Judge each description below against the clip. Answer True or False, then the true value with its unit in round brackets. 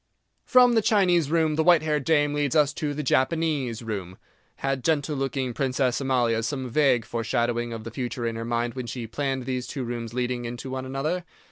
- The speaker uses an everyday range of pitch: True (3.9 semitones)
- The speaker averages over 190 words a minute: True (200 wpm)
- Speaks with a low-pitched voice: True (130 Hz)